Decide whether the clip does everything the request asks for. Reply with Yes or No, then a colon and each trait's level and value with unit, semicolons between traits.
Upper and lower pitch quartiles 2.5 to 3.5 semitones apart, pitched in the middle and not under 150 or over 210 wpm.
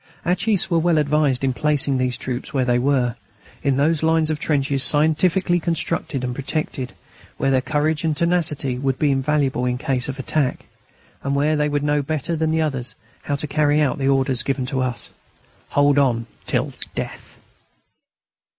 Yes: average, 2.8 semitones; medium, 145 Hz; average, 180 wpm